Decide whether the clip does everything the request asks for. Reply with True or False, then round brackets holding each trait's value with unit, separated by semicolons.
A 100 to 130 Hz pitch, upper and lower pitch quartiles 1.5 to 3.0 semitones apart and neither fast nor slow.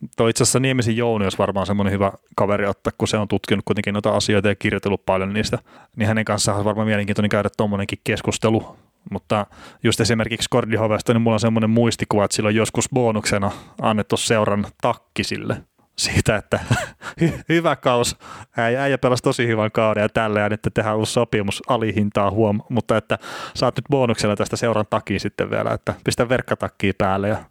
False (110 Hz; 2.4 semitones; 175 wpm)